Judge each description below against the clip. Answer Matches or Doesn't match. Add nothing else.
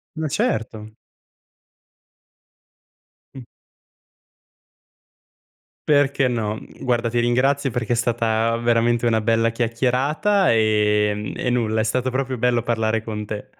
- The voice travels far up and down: Doesn't match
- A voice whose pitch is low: Matches